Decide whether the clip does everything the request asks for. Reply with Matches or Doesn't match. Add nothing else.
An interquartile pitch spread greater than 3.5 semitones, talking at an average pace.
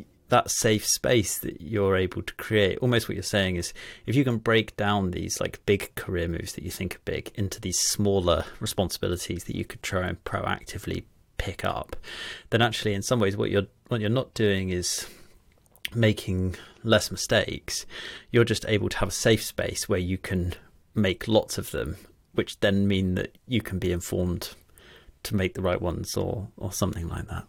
Doesn't match